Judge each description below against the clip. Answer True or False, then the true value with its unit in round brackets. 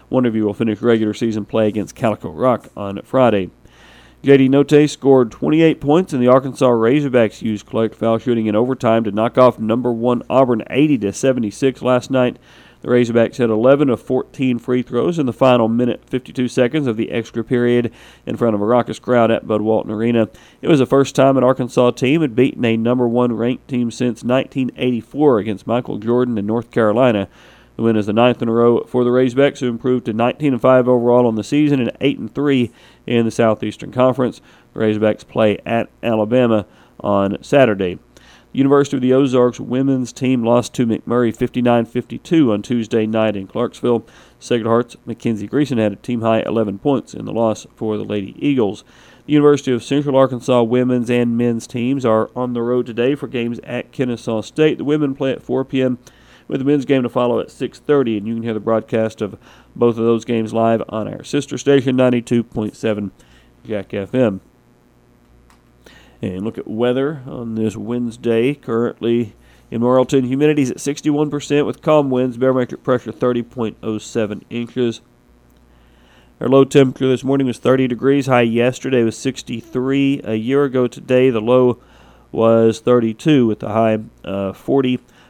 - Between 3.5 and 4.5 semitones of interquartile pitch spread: False (2.7 semitones)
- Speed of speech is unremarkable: True (190 wpm)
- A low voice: True (120 Hz)